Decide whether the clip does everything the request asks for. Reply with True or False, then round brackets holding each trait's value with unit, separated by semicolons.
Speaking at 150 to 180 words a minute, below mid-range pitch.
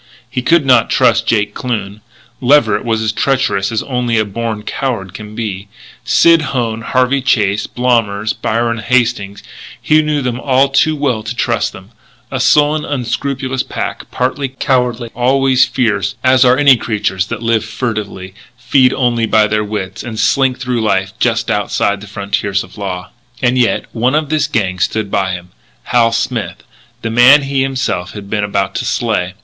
True (170 wpm; 115 Hz)